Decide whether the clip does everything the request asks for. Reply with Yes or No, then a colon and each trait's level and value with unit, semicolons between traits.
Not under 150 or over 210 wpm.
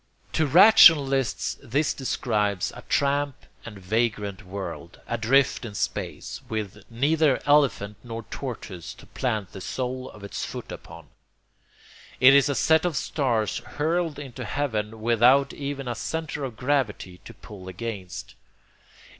No: slow, 135 wpm